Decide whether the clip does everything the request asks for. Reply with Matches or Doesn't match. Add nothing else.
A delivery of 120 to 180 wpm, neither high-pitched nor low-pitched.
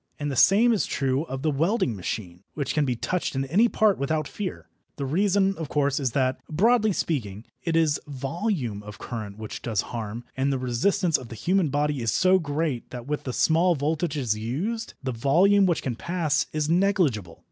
Doesn't match